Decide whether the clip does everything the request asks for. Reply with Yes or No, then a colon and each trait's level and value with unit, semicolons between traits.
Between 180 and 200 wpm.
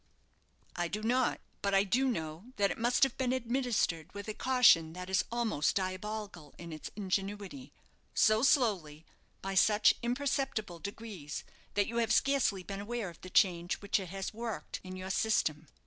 No: average, 170 wpm